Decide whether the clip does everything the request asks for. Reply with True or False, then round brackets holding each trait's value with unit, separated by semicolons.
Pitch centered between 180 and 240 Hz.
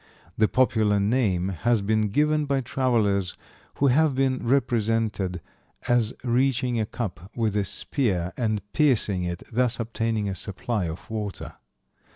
False (110 Hz)